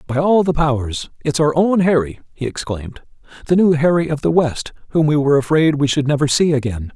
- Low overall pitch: No, medium, 145 Hz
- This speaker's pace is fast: Yes, fast, 215 wpm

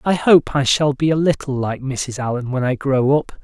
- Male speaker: Yes, male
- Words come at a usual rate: No, fast, 245 wpm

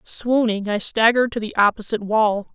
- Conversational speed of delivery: Yes, average, 165 wpm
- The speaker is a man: No, female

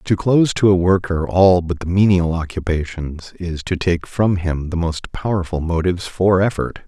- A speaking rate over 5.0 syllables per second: No, 4.8 syllables/s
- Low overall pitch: Yes, very low, 90 Hz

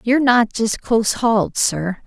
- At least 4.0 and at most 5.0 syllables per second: Yes, 4.6 syllables/s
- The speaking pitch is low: No, high, 230 Hz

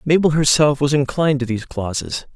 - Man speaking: Yes, male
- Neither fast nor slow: Yes, average, 180 wpm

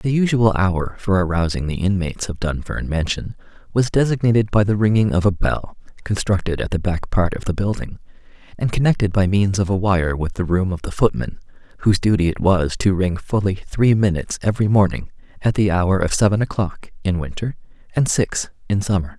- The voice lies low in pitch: Yes, very low, 95 Hz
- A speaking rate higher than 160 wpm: Yes, average, 195 wpm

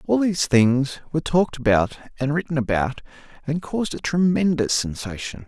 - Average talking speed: Yes, average, 155 wpm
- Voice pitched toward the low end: No, medium, 145 Hz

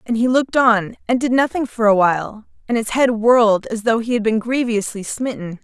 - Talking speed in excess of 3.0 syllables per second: Yes, 5.4 syllables/s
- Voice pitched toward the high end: Yes, high, 230 Hz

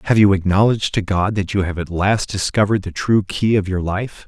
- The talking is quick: Yes, fast, 240 wpm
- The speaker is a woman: No, male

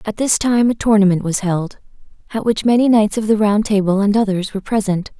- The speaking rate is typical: No, fast, 220 wpm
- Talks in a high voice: Yes, high, 210 Hz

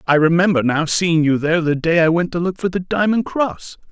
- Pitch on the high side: No, medium, 170 Hz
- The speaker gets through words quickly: Yes, fast, 245 wpm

